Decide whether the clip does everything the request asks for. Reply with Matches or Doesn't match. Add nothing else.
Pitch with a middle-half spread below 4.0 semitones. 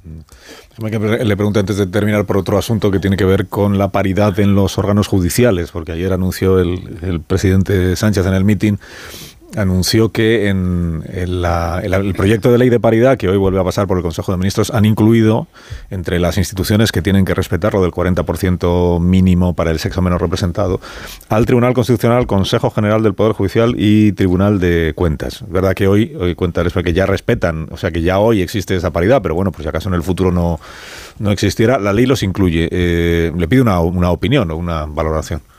Matches